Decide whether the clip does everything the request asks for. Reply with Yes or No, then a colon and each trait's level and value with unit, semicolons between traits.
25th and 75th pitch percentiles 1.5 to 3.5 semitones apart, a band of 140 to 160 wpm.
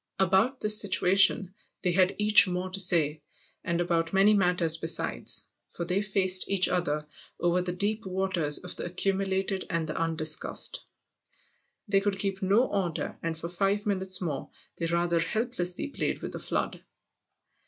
Yes: narrow, 2.4 semitones; average, 155 wpm